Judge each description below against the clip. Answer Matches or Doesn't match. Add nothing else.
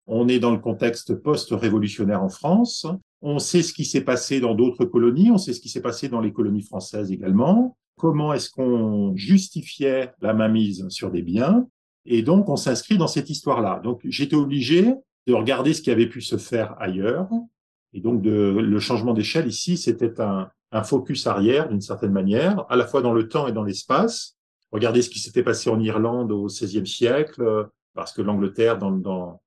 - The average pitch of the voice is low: Matches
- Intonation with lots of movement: Matches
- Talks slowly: Doesn't match